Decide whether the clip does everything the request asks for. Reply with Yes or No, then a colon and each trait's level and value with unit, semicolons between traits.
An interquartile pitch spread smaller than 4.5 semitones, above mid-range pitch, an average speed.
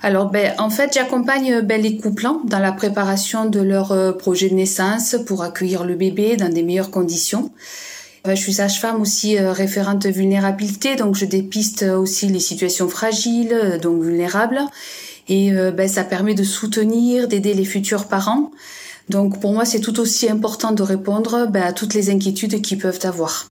Yes: narrow, 2.6 semitones; high, 200 Hz; average, 175 wpm